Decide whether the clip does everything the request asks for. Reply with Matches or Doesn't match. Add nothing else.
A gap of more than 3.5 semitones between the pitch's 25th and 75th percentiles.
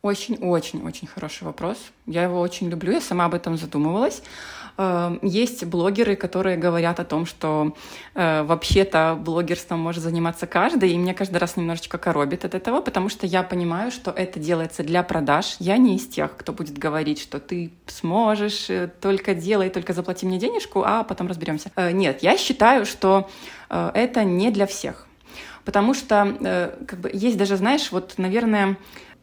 Doesn't match